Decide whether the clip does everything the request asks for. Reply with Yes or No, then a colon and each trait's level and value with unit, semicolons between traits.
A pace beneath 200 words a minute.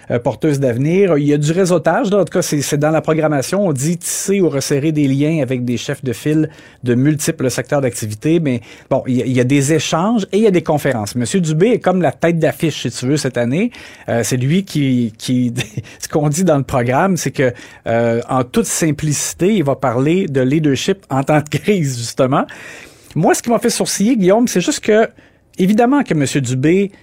No: fast, 220 wpm